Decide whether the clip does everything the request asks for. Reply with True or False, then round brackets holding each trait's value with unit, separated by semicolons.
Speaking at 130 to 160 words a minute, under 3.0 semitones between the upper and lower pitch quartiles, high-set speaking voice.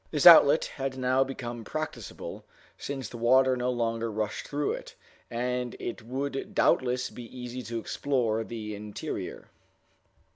False (140 wpm; 2.4 semitones; 125 Hz)